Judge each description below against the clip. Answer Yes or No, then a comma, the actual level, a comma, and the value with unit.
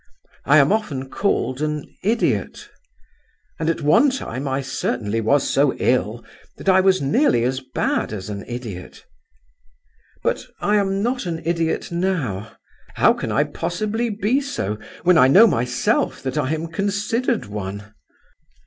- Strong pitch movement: Yes, wide, 8.2 semitones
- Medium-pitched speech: Yes, medium, 150 Hz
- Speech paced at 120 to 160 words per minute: Yes, average, 150 wpm